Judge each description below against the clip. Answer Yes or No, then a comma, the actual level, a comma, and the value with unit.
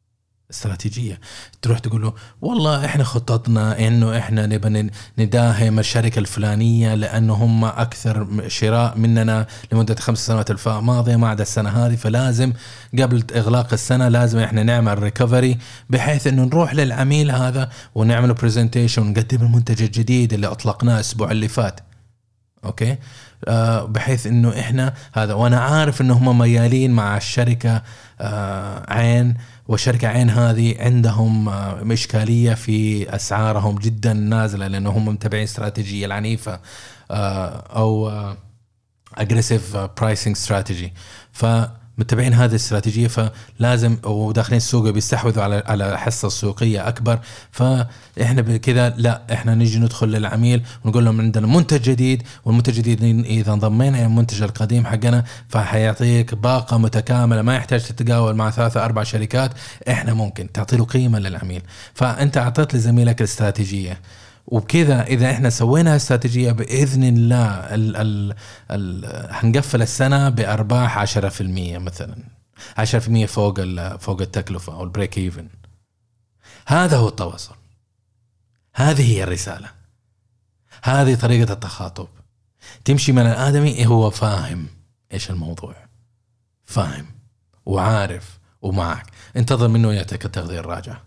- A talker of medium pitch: No, low, 115 Hz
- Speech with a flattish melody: Yes, narrow, 2.2 semitones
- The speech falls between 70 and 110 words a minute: No, average, 120 wpm